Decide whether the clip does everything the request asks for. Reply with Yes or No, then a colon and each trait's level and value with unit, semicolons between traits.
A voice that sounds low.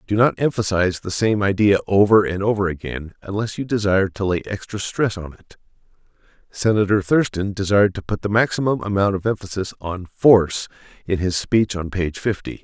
Yes: low, 100 Hz